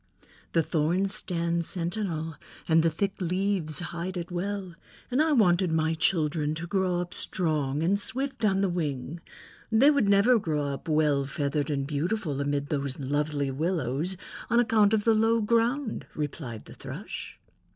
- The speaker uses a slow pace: No, average, 160 wpm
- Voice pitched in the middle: Yes, medium, 170 Hz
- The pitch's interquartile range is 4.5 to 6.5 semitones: Yes, average, 5.0 semitones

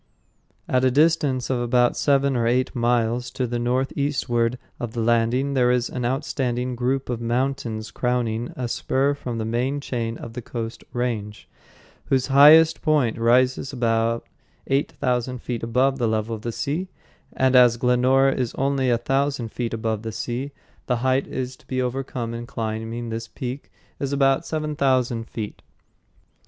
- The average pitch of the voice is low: Yes, low, 125 Hz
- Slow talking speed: No, average, 165 wpm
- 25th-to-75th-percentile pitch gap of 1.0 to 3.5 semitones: Yes, narrow, 2.4 semitones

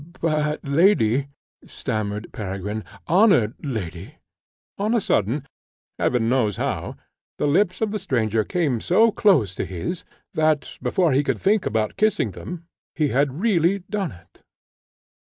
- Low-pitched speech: No, medium, 145 Hz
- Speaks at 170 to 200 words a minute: No, average, 140 wpm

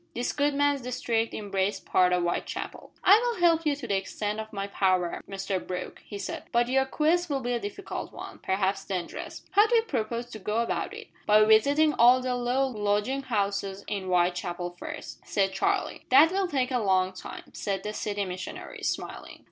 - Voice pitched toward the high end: Yes, high, 215 Hz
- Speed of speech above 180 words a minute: Yes, average, 195 wpm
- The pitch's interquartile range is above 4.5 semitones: Yes, wide, 5.6 semitones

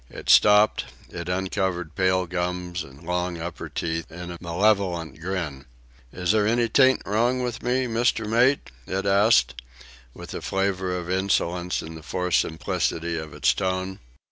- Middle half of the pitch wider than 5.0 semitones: No, average, 3.3 semitones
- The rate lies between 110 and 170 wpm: Yes, average, 155 wpm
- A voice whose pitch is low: Yes, very low, 90 Hz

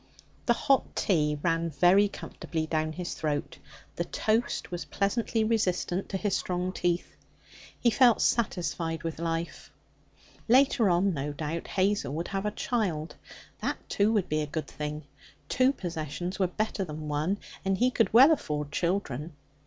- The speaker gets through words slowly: No, average, 155 wpm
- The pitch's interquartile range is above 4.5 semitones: Yes, average, 4.9 semitones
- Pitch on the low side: No, medium, 180 Hz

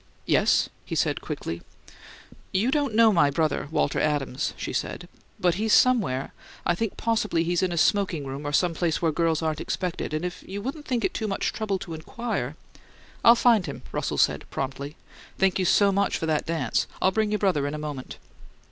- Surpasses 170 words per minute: Yes, average, 200 wpm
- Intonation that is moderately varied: No, wide, 5.7 semitones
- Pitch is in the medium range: Yes, medium, 175 Hz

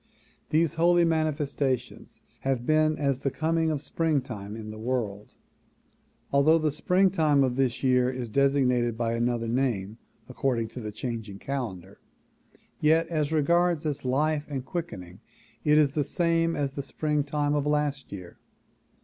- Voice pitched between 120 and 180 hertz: Yes, medium, 140 Hz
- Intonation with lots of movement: No, average, 4.3 semitones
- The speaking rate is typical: Yes, average, 145 wpm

